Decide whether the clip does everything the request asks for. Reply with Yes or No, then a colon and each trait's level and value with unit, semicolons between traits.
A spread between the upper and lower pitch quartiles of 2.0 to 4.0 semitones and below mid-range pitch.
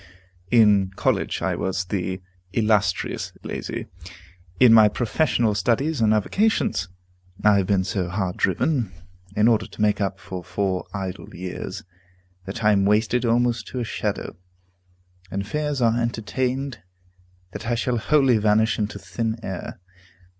Yes: average, 3.5 semitones; low, 105 Hz